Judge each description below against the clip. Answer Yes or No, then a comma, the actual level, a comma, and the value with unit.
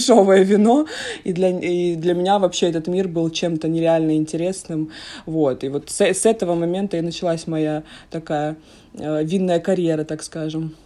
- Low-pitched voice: No, medium, 170 Hz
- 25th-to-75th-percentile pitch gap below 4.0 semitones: Yes, average, 2.9 semitones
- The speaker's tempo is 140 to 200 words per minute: Yes, fast, 160 wpm